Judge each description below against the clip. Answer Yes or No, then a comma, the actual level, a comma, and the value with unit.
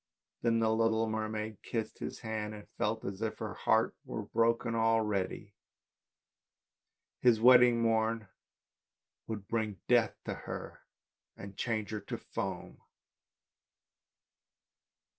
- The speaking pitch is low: Yes, low, 110 Hz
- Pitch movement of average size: No, narrow, 1.2 semitones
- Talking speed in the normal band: No, slow, 115 wpm